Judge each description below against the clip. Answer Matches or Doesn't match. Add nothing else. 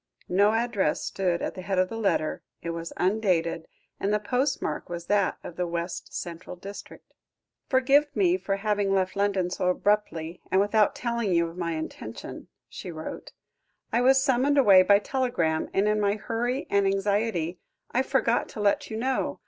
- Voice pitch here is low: Doesn't match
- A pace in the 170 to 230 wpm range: Matches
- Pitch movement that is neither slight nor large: Matches